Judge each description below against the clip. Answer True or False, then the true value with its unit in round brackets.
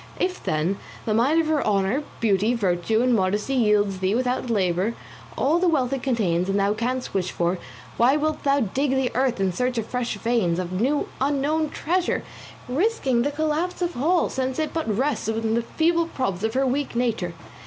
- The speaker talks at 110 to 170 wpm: False (195 wpm)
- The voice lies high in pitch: True (245 Hz)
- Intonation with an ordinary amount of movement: False (5.8 semitones)